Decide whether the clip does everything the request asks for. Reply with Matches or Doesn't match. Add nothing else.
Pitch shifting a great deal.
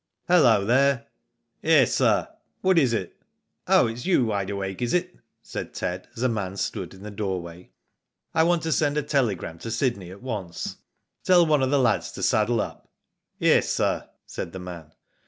Matches